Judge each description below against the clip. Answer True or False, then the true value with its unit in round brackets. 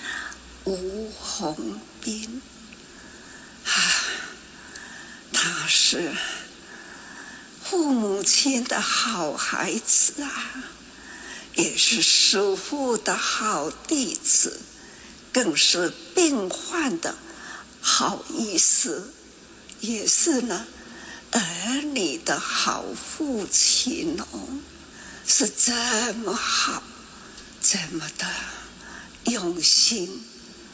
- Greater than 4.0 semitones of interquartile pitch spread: True (5.3 semitones)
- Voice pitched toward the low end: False (250 Hz)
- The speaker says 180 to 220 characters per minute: False (95 characters per minute)